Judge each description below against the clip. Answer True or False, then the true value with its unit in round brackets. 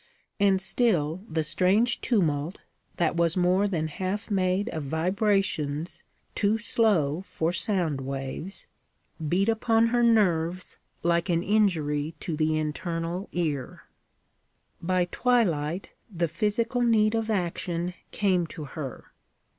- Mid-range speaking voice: True (180 Hz)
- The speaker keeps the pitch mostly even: False (4.4 semitones)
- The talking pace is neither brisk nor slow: False (120 wpm)